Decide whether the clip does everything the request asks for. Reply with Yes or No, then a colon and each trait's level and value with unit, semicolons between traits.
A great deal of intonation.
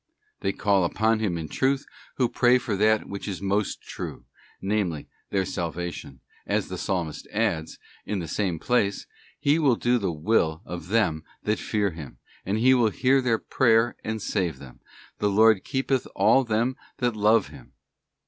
No: average, 4.3 semitones